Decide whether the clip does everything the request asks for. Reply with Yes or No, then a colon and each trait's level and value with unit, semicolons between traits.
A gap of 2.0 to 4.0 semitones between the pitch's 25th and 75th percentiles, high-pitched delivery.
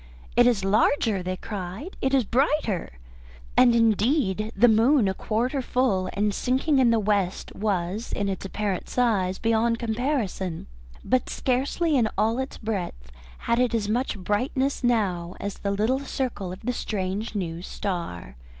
No: average, 4.5 semitones; high, 220 Hz